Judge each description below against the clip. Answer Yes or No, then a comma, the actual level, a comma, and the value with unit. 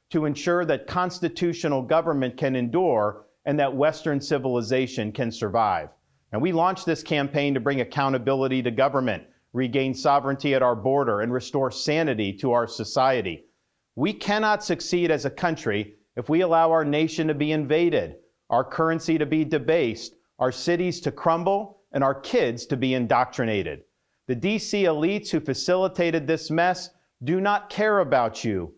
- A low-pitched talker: No, medium, 145 Hz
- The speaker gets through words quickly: No, average, 155 wpm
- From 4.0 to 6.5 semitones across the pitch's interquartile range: Yes, average, 4.5 semitones